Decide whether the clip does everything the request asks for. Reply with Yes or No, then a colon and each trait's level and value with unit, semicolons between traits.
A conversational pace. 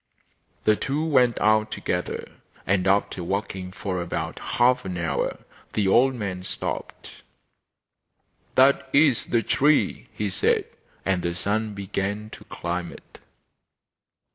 No: slow, 125 wpm